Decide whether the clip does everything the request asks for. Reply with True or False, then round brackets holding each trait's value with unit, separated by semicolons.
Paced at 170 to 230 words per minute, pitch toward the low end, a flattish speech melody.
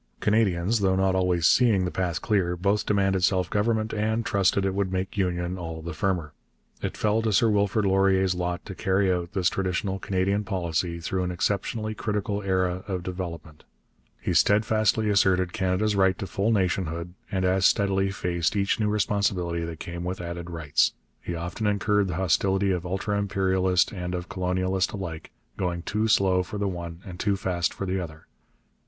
True (180 wpm; 95 Hz; 2.2 semitones)